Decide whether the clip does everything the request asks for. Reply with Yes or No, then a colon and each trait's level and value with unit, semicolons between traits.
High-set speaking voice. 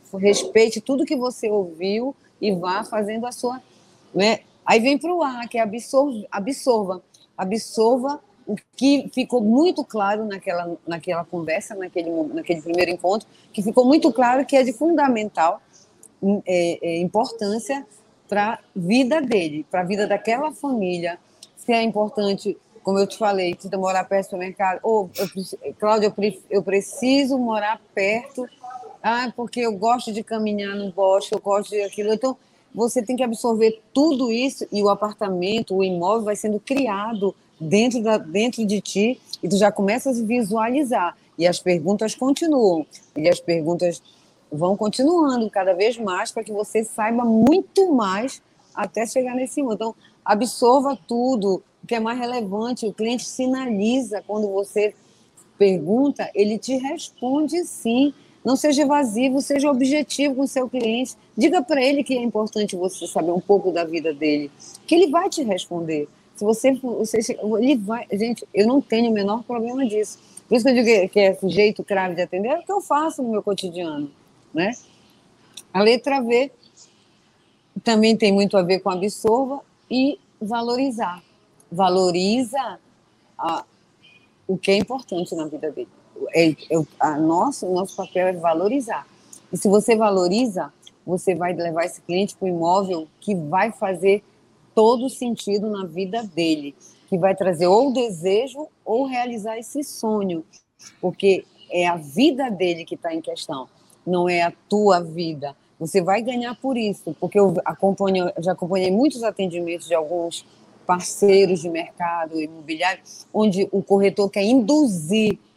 Yes: high, 210 Hz